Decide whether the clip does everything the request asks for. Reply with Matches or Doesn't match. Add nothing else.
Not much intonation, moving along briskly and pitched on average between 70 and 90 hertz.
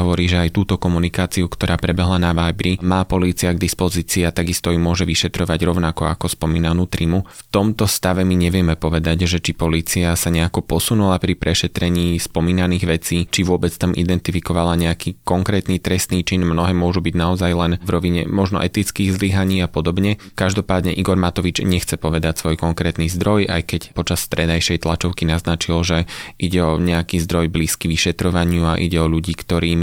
Matches